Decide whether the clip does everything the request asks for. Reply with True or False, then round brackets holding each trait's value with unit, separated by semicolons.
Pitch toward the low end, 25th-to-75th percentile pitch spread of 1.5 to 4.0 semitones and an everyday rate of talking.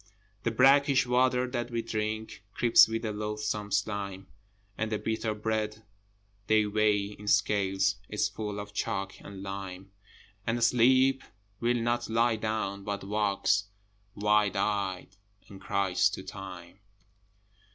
False (105 Hz; 2.4 semitones; 130 wpm)